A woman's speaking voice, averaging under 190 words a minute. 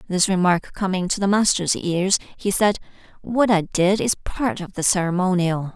Yes: female; average, 175 wpm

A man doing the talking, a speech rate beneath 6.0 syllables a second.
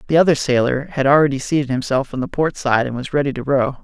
No: male; 6.4 syllables/s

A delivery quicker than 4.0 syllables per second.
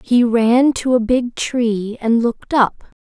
No: 3.6 syllables/s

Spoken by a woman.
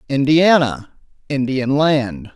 No: male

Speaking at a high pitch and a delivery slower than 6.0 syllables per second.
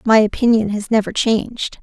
Yes: high, 220 Hz; 5.4 syllables/s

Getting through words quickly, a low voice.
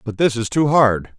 Yes: fast, 255 wpm; low, 120 Hz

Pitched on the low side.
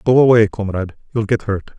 Yes: low, 110 Hz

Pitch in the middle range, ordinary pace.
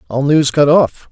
No: medium, 145 Hz; fast, 215 wpm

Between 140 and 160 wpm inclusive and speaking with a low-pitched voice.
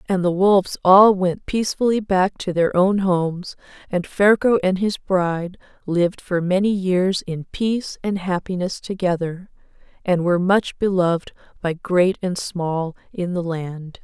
No: average, 155 wpm; medium, 185 Hz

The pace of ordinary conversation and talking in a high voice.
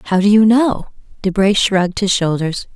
Yes: average, 175 wpm; high, 200 Hz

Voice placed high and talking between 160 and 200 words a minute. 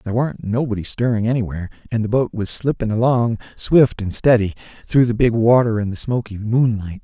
No: low, 115 Hz; average, 190 wpm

